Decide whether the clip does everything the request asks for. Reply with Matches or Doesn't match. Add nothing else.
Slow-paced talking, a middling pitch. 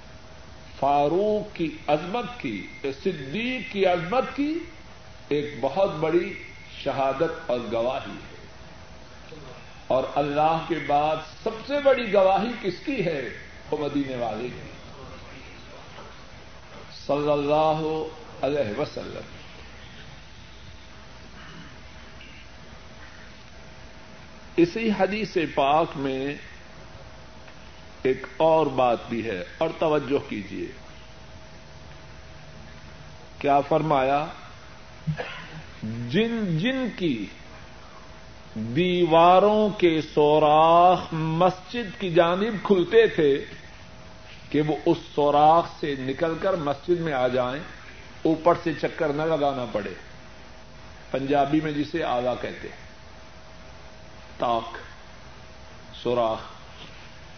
Matches